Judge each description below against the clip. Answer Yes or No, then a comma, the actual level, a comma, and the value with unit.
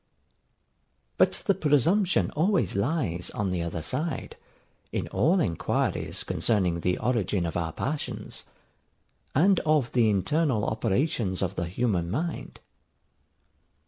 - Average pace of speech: No, slow, 115 wpm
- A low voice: Yes, low, 115 Hz